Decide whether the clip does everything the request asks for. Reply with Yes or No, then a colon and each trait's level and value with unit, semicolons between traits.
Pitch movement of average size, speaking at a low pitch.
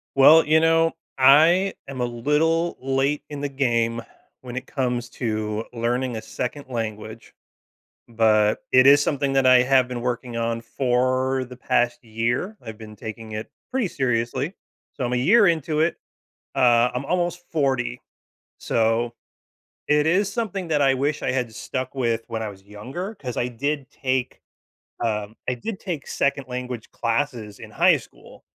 Yes: average, 3.9 semitones; low, 130 Hz